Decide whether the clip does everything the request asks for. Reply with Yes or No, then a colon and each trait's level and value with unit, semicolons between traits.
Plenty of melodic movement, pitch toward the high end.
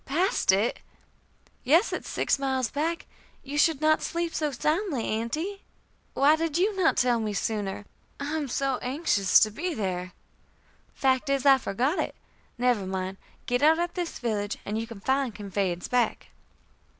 Yes: wide, 6.4 semitones; very high, 265 Hz